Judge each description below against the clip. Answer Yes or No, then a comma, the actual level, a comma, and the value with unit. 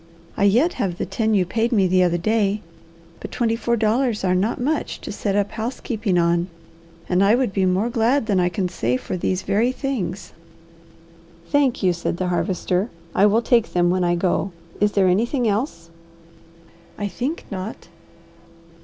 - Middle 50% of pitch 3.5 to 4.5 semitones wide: Yes, average, 4.1 semitones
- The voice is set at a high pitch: Yes, high, 200 Hz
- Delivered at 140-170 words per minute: No, average, 180 wpm